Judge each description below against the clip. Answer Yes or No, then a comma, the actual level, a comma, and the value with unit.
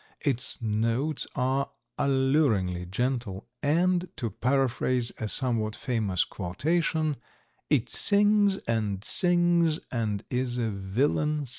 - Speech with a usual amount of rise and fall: No, wide, 5.7 semitones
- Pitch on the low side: Yes, low, 130 Hz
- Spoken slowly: Yes, slow, 110 wpm